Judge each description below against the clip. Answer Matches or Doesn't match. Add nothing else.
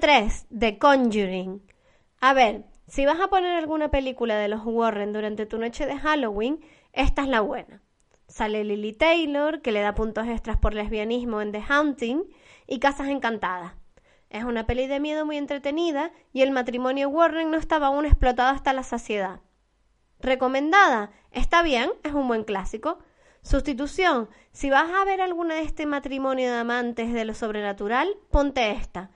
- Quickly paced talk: Doesn't match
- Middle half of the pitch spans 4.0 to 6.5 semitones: Matches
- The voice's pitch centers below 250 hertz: Doesn't match